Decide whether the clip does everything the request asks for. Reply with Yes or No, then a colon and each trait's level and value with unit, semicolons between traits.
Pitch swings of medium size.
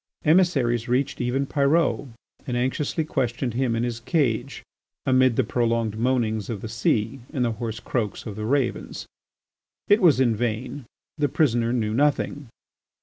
Yes: average, 3.3 semitones